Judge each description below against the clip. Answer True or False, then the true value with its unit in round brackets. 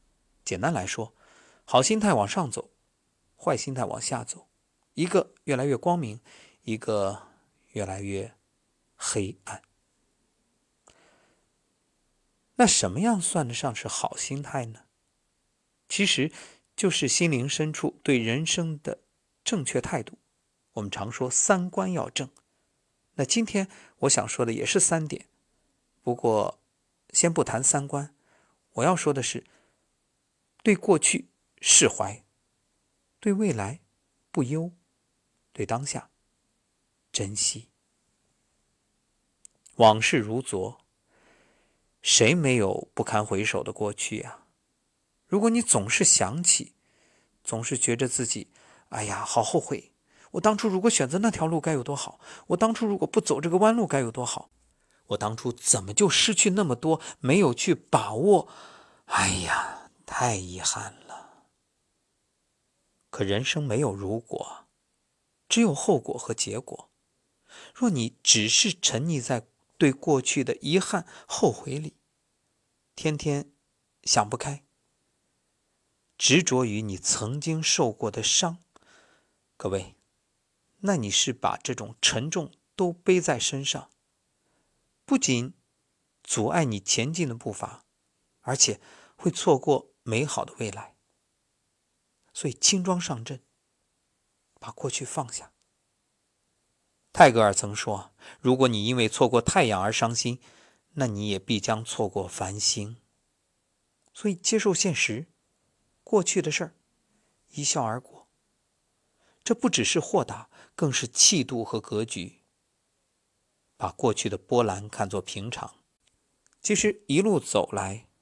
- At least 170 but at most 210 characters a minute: True (180 characters per minute)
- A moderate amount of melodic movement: False (7.9 semitones)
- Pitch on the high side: False (135 Hz)